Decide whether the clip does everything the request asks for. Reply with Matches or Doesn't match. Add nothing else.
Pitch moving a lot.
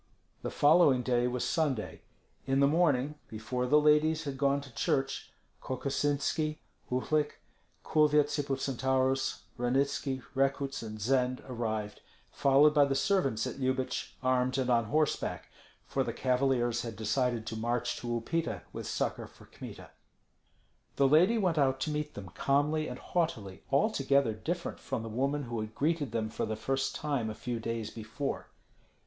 Doesn't match